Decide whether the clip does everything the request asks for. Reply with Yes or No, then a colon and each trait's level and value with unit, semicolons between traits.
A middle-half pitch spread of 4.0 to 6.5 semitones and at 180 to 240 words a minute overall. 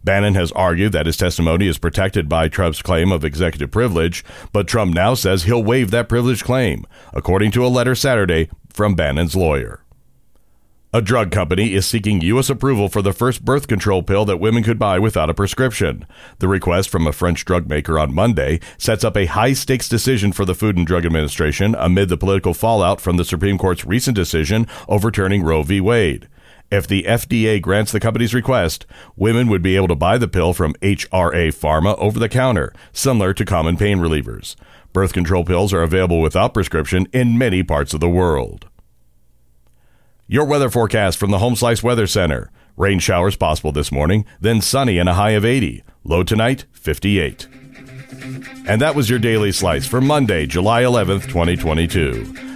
Yes: average, 4.9 semitones; average, 185 wpm